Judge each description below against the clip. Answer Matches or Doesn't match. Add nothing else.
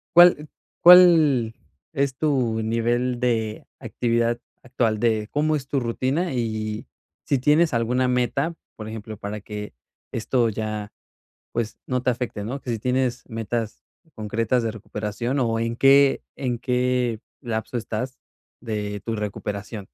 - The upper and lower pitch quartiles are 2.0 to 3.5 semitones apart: Matches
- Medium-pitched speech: Doesn't match